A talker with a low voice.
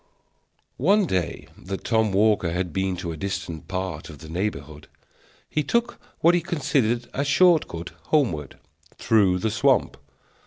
Yes: low, 100 Hz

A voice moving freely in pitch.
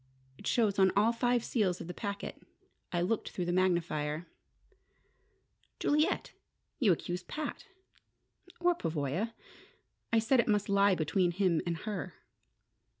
No: average, 4.5 semitones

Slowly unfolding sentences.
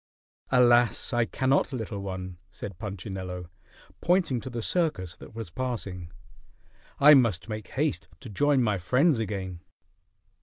Yes: slow, 130 wpm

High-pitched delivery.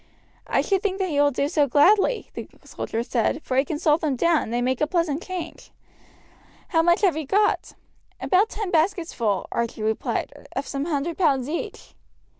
Yes: very high, 310 Hz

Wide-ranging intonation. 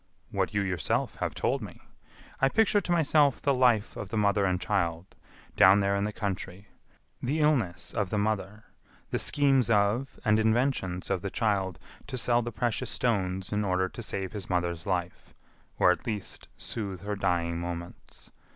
No: average, 4.2 semitones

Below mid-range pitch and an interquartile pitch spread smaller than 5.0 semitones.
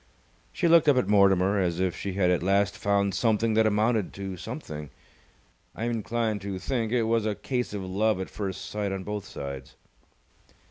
Yes: low, 100 Hz; average, 3.0 semitones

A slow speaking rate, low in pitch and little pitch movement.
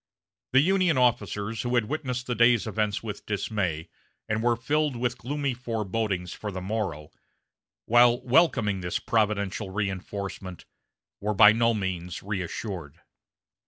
No: slow, 130 wpm; low, 110 Hz; average, 4.0 semitones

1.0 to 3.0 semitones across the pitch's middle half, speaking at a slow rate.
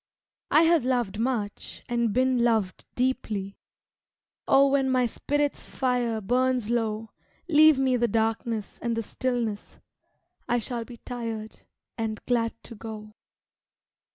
Yes: average, 2.7 semitones; slow, 125 wpm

